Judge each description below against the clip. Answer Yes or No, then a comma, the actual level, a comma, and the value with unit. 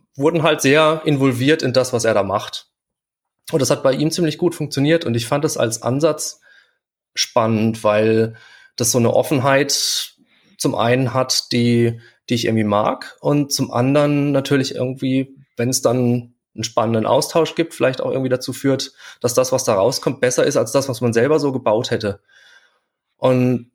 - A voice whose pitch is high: No, low, 130 Hz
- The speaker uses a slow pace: No, average, 180 wpm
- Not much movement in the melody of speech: No, average, 3.4 semitones